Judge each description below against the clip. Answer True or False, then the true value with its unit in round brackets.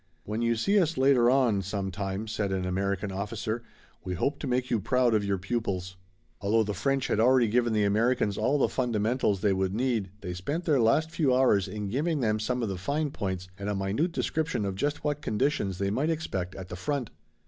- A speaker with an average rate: False (215 wpm)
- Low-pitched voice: True (110 Hz)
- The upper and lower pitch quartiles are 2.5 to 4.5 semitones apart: False (5.0 semitones)